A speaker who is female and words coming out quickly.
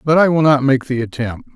No: male; fast, 270 wpm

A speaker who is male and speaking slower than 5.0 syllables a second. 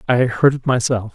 No: male; 5.1 syllables/s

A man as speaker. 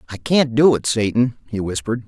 Yes: male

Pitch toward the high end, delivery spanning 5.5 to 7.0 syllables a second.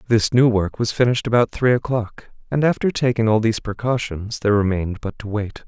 No: low, 115 Hz; 5.9 syllables/s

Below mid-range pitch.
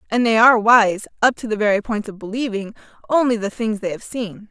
No: high, 220 Hz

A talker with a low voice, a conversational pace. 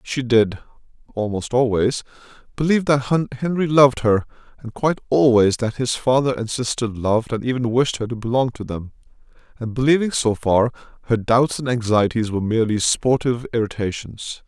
Yes: low, 120 Hz; average, 150 wpm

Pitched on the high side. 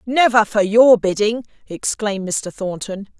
Yes: high, 215 Hz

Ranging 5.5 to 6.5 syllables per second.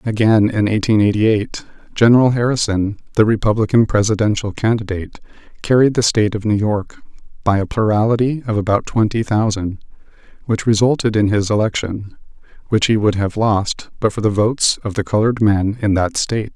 Yes: 5.6 syllables/s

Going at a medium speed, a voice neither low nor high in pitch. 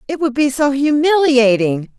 No: average, 150 wpm; very high, 275 Hz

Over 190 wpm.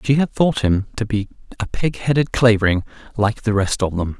Yes: average, 200 wpm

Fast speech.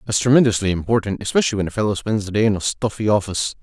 Yes: fast, 230 wpm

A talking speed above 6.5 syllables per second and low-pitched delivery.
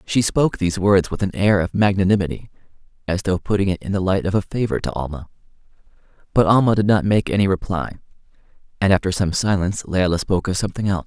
Yes: 6.7 syllables/s; very low, 95 Hz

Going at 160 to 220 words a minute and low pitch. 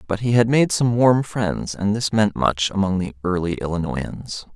Yes: average, 200 wpm; low, 100 Hz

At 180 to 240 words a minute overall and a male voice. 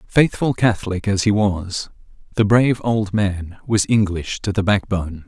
No: average, 160 wpm; male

